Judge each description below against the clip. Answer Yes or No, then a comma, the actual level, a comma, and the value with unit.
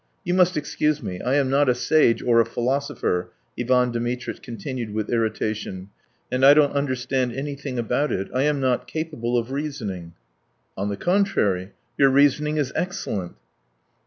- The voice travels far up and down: No, average, 3.8 semitones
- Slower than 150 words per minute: No, average, 160 wpm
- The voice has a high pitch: No, low, 130 Hz